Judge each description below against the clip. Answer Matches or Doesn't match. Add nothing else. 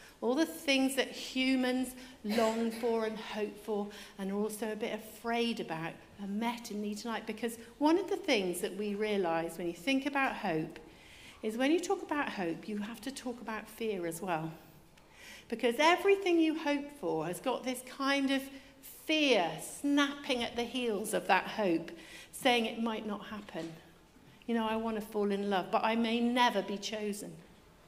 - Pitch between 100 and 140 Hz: Doesn't match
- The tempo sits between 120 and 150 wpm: Doesn't match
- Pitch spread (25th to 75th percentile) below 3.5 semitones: Doesn't match